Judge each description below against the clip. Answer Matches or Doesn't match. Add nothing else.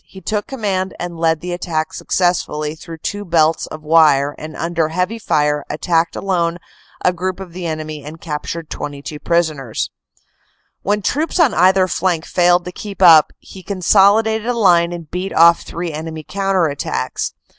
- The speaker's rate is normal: Matches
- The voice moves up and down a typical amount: Matches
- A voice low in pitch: Doesn't match